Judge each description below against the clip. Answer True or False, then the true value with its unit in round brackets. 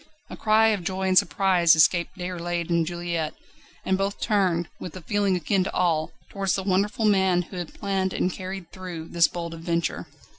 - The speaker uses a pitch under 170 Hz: False (185 Hz)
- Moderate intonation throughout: False (2.2 semitones)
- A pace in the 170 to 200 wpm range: True (185 wpm)